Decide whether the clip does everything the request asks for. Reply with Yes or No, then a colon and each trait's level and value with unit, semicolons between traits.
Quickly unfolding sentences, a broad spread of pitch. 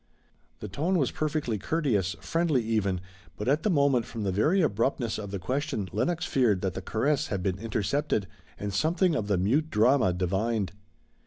No: average, 175 wpm; wide, 6.8 semitones